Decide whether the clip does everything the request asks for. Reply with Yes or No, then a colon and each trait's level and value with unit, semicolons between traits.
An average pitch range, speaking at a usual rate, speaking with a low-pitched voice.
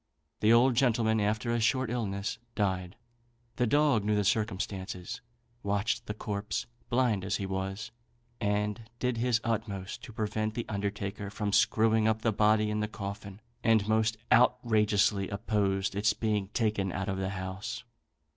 No: narrow, 2.2 semitones; average, 155 wpm; low, 105 Hz